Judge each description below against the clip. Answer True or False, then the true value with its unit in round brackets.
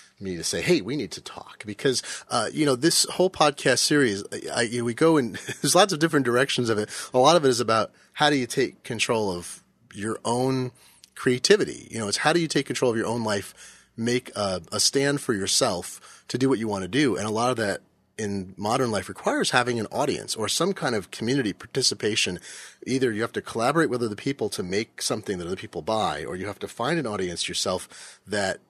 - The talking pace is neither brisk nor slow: False (235 wpm)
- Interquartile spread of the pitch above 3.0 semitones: True (4.2 semitones)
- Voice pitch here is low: True (125 Hz)